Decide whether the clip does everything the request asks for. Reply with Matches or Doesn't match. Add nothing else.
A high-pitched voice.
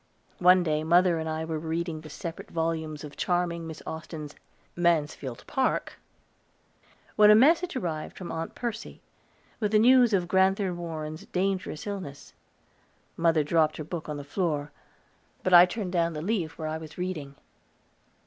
Doesn't match